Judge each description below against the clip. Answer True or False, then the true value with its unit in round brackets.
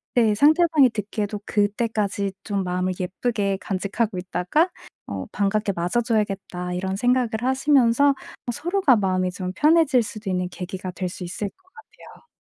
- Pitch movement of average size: True (4.9 semitones)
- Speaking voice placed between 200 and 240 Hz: True (205 Hz)